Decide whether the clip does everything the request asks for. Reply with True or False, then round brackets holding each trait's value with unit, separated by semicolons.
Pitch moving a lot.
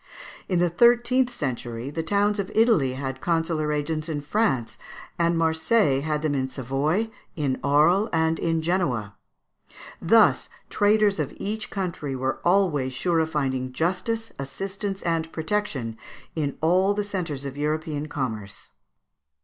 True (5.8 semitones)